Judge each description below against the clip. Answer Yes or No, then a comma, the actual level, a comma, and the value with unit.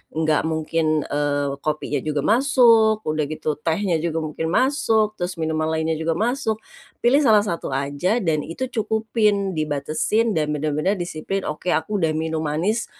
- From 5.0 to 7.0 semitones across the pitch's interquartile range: Yes, wide, 5.6 semitones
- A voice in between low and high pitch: Yes, medium, 160 Hz